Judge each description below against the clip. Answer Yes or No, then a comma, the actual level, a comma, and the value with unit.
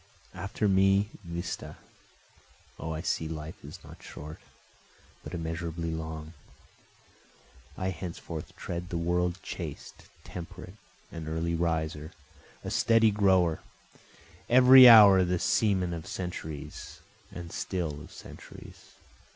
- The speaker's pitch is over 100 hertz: No, very low, 85 Hz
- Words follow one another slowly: Yes, slow, 110 wpm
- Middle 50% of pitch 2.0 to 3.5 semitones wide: Yes, average, 2.8 semitones